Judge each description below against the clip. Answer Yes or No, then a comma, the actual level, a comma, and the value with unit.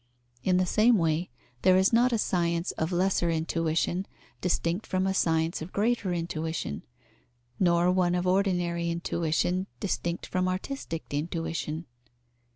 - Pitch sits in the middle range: Yes, medium, 175 Hz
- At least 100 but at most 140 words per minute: Yes, slow, 135 wpm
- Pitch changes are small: Yes, narrow, 2.1 semitones